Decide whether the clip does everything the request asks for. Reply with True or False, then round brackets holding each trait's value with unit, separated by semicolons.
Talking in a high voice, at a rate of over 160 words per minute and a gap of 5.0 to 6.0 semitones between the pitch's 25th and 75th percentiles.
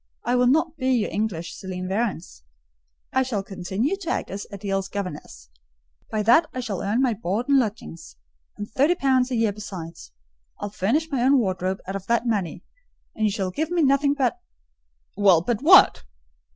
True (215 Hz; 180 wpm; 5.3 semitones)